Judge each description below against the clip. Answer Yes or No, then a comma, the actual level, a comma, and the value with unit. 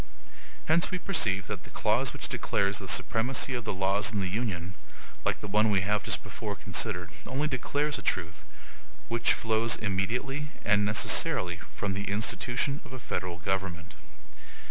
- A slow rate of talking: No, average, 165 wpm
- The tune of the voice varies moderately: Yes, average, 4.4 semitones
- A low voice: Yes, low, 105 Hz